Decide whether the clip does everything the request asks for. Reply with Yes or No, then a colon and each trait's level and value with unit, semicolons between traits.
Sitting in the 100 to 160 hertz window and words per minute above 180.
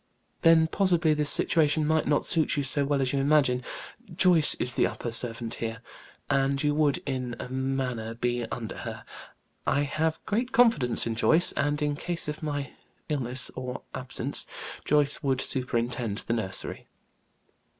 No: medium, 140 Hz; average, 160 wpm